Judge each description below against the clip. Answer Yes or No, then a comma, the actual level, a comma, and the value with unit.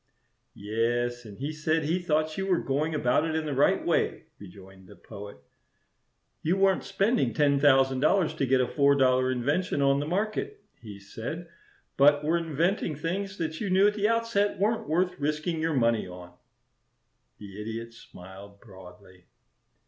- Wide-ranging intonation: Yes, wide, 6.9 semitones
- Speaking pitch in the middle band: Yes, medium, 145 Hz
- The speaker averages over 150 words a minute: Yes, average, 165 wpm